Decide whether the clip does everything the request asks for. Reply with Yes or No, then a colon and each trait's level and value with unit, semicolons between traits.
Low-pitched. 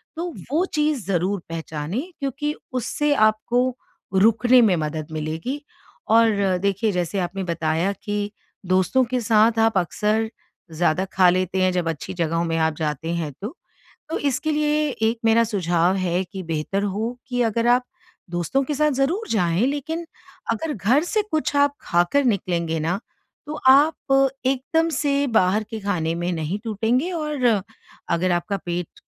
No: high, 205 Hz